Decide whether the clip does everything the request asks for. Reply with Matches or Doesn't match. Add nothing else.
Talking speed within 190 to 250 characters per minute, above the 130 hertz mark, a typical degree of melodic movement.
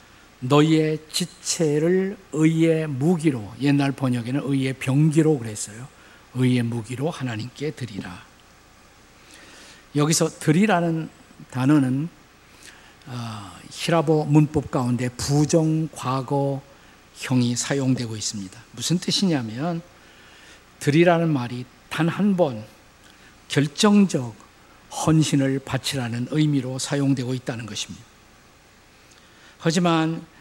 Matches